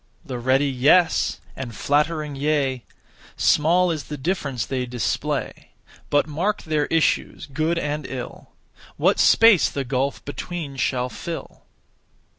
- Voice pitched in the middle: Yes, medium, 145 Hz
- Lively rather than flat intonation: No, average, 3.5 semitones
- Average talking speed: No, slow, 125 wpm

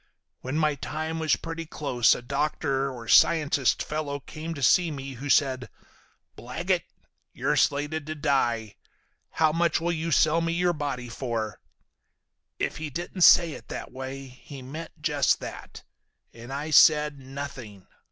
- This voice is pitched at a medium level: Yes, medium, 145 Hz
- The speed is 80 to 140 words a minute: No, average, 150 wpm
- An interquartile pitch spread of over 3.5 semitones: No, average, 3.2 semitones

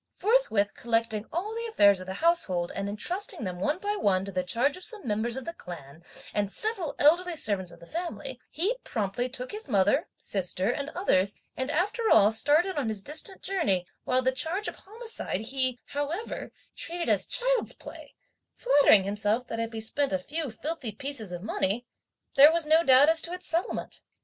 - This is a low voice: No, very high, 260 Hz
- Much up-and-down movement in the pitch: Yes, wide, 8.7 semitones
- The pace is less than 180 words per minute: No, average, 190 wpm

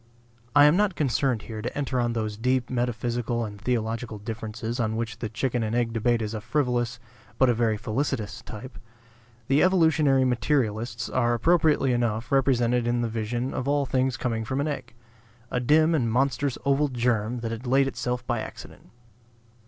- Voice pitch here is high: No, low, 120 Hz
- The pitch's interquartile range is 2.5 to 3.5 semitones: Yes, average, 2.9 semitones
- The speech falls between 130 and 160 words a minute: No, average, 175 wpm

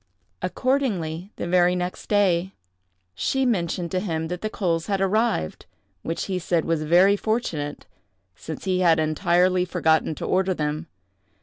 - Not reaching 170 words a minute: Yes, average, 140 wpm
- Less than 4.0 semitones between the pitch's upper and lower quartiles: Yes, average, 3.3 semitones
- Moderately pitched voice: Yes, medium, 180 Hz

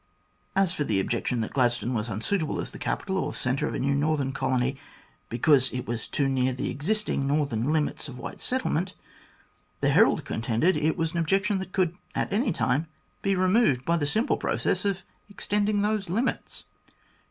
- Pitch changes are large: Yes, wide, 7.0 semitones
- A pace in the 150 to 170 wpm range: No, average, 185 wpm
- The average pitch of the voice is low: No, medium, 155 Hz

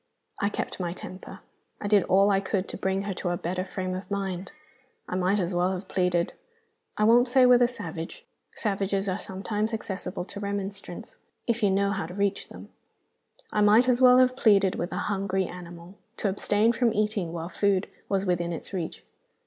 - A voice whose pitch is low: No, high, 195 Hz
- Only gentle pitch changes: Yes, narrow, 2.3 semitones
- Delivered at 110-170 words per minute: No, average, 195 wpm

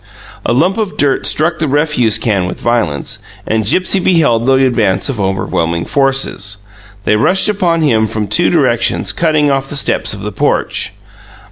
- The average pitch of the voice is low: Yes, low, 130 Hz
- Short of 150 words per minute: No, average, 165 wpm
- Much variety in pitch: Yes, wide, 6.6 semitones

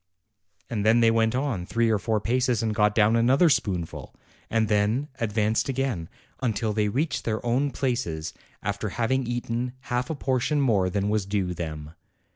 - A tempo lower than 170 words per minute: No, average, 175 wpm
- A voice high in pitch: No, low, 115 Hz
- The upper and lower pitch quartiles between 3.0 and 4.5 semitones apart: Yes, average, 3.3 semitones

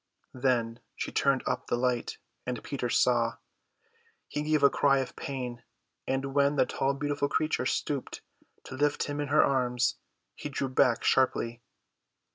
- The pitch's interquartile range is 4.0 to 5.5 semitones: No, narrow, 2.5 semitones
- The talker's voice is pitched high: No, low, 135 Hz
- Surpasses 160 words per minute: No, average, 155 wpm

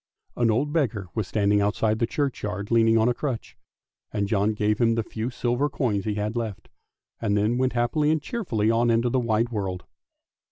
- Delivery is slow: No, average, 195 wpm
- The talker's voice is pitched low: Yes, low, 115 Hz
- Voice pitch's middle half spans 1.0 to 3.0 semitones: Yes, average, 2.7 semitones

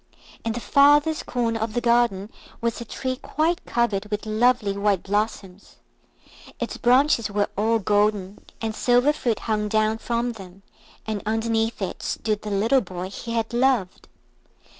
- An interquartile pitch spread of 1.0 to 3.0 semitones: Yes, average, 2.7 semitones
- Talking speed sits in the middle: Yes, average, 155 wpm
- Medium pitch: No, high, 225 Hz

